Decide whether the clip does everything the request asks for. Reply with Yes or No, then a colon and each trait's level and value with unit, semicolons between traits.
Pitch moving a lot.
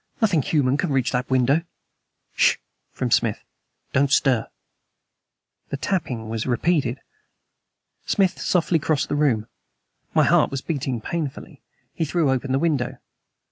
No: average, 4.2 semitones